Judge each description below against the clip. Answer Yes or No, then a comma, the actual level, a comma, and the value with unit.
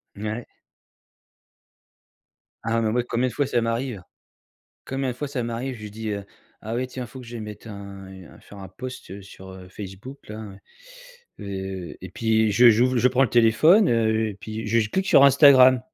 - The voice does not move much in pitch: No, average, 3.8 semitones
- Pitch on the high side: No, low, 115 Hz